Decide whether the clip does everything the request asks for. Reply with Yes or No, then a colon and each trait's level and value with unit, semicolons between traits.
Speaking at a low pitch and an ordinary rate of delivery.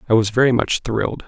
No: low, 115 Hz; fast, 235 wpm